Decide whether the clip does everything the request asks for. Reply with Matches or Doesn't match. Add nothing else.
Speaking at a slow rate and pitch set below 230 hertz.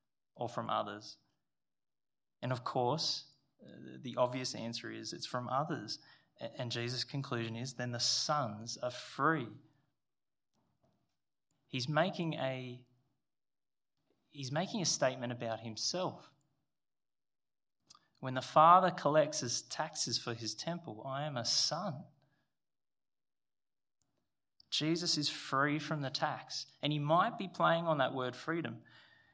Matches